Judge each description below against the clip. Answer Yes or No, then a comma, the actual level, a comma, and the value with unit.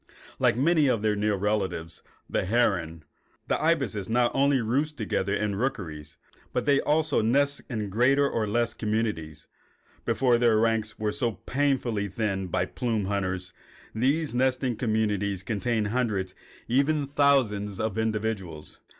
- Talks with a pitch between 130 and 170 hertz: No, low, 110 Hz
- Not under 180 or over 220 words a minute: No, average, 145 wpm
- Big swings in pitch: No, average, 4.2 semitones